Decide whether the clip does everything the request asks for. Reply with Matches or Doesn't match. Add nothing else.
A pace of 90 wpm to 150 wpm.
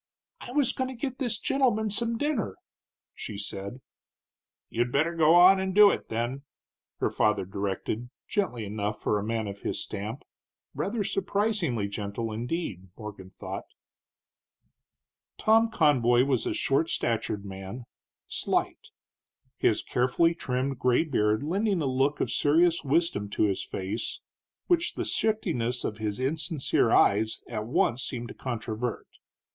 Matches